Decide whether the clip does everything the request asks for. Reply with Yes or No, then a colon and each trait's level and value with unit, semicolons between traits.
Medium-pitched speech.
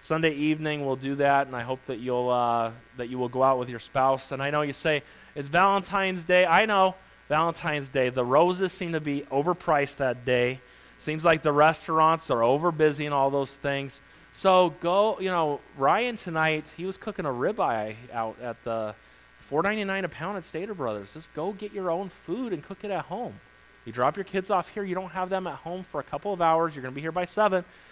Yes: medium, 155 Hz